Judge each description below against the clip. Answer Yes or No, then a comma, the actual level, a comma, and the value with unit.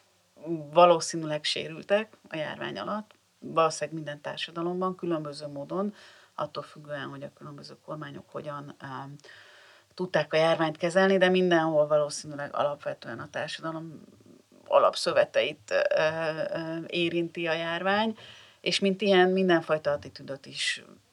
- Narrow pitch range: No, average, 3.3 semitones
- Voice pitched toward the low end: No, medium, 165 Hz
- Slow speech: No, average, 115 wpm